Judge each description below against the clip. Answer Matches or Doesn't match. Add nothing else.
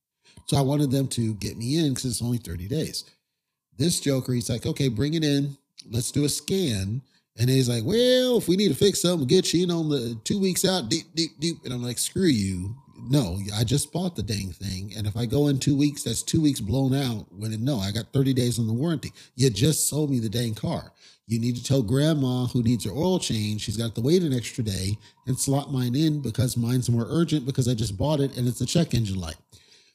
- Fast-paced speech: Matches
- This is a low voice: Matches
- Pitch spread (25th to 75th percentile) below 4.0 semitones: Doesn't match